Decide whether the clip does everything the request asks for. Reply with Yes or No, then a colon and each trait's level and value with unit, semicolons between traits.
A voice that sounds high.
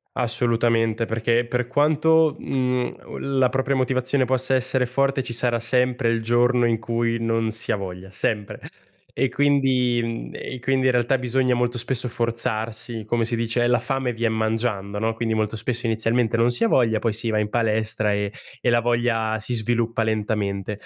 No: low, 120 Hz